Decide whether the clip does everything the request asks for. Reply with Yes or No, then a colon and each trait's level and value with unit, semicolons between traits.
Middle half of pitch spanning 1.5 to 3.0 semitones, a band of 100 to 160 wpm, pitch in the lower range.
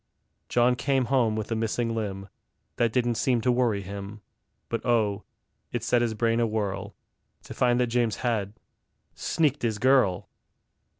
Yes: narrow, 2.5 semitones; average, 155 wpm; low, 115 Hz